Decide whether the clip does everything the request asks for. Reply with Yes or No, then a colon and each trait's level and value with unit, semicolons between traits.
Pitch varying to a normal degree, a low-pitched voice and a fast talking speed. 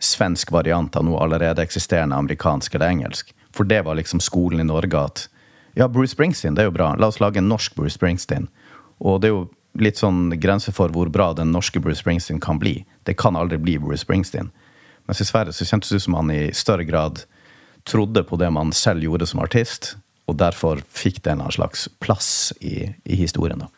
Yes: average, 3.8 semitones; very low, 90 Hz; fast, 210 wpm